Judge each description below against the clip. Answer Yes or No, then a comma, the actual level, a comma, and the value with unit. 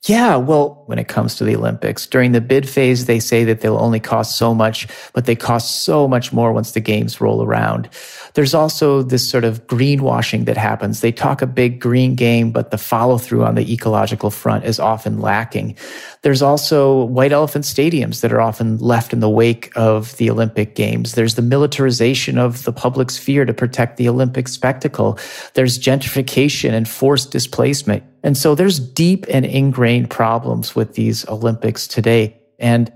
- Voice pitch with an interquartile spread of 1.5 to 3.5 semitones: Yes, average, 2.9 semitones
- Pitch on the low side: Yes, low, 120 Hz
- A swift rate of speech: No, average, 185 wpm